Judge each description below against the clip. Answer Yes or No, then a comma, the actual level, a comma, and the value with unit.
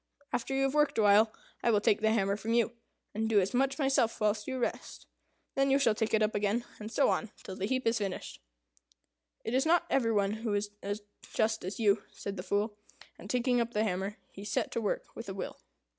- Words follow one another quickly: Yes, fast, 230 wpm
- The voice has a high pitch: Yes, high, 220 Hz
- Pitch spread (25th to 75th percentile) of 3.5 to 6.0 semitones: No, average, 2.9 semitones